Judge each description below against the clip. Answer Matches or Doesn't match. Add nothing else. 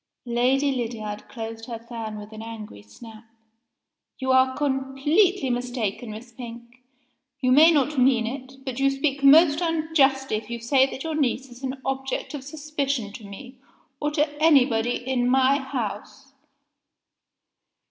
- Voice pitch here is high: Matches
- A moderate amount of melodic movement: Matches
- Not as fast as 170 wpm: Matches